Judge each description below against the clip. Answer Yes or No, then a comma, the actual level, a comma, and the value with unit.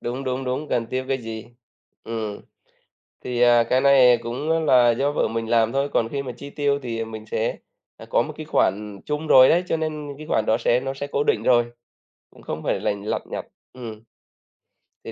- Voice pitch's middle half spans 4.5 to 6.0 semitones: No, average, 3.7 semitones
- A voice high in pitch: No, low, 125 Hz